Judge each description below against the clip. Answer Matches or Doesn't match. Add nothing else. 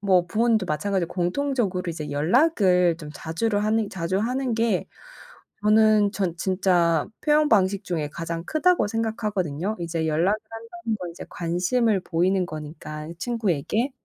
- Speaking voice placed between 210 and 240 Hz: Doesn't match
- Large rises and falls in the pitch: Doesn't match